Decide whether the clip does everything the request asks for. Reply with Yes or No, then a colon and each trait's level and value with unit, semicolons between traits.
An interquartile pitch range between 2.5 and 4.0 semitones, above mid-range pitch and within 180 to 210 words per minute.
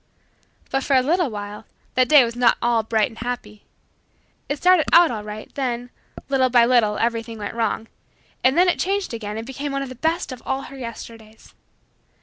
Yes: average, 3.5 semitones; high, 245 Hz; average, 200 wpm